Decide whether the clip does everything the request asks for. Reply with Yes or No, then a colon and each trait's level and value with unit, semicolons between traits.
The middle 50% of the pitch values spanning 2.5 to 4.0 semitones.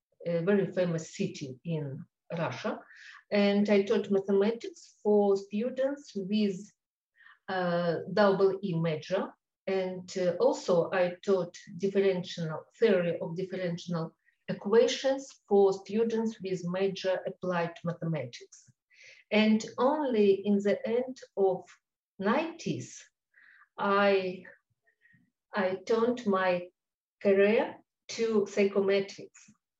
Yes: average, 2.9 semitones